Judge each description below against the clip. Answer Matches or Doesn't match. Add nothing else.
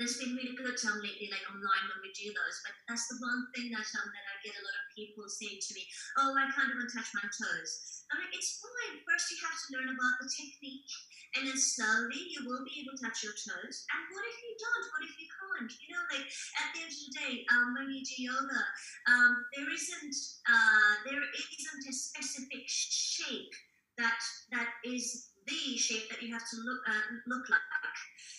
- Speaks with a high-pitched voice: Matches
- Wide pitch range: Doesn't match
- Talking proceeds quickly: Matches